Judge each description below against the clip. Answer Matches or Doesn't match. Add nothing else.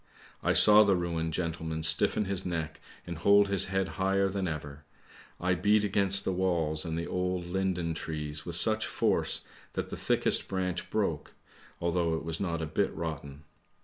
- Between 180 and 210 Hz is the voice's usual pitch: Doesn't match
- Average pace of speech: Matches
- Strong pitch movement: Doesn't match